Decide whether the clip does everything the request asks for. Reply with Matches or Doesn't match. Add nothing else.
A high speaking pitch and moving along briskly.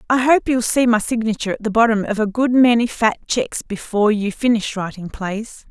Matches